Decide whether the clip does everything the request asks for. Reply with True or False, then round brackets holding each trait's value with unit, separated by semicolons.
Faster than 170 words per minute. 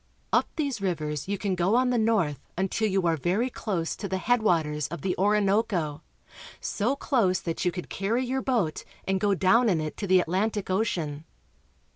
True (195 wpm)